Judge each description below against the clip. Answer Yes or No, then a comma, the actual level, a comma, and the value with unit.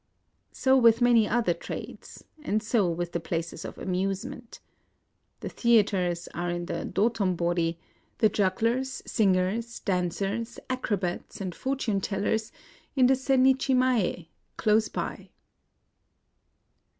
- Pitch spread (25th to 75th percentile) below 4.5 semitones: No, average, 4.8 semitones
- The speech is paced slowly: Yes, slow, 115 wpm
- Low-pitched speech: No, high, 210 Hz